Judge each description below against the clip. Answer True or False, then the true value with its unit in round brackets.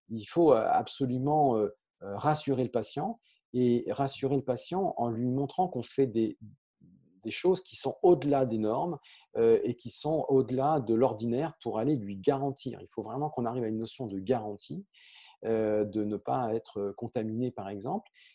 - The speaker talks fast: False (165 wpm)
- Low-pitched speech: True (125 Hz)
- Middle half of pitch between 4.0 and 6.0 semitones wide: True (4.3 semitones)